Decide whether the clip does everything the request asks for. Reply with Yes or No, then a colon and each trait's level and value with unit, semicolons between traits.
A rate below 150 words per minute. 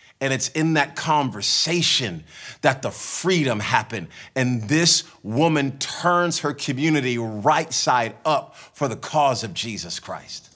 Yes: slow, 135 wpm